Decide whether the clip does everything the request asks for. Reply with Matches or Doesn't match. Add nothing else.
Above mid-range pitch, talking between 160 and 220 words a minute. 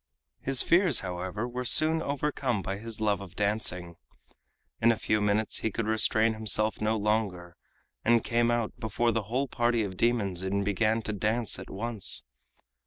Doesn't match